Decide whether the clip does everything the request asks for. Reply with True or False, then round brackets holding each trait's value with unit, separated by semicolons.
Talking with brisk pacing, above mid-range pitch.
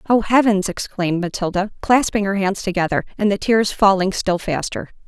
False (165 wpm; 200 Hz)